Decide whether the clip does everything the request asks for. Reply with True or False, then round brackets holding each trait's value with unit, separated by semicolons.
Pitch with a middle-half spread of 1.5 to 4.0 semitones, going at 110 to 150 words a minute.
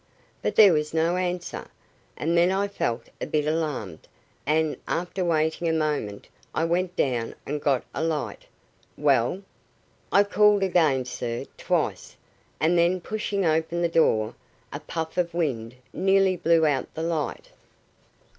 True (3.2 semitones; 145 wpm)